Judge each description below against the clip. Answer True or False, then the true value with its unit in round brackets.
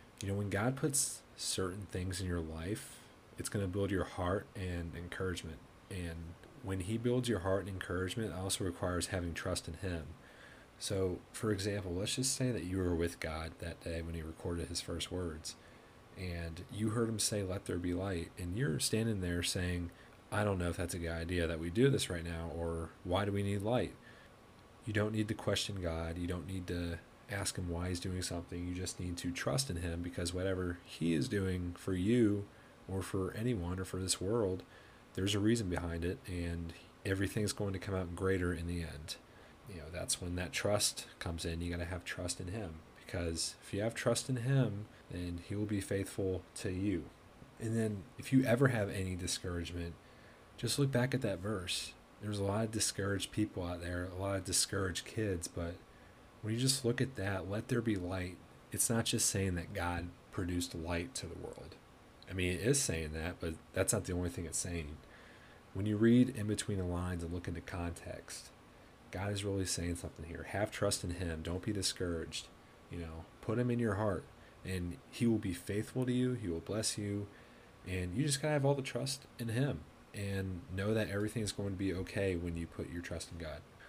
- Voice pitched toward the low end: True (95 Hz)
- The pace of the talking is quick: True (215 wpm)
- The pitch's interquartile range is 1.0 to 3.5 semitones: False (3.9 semitones)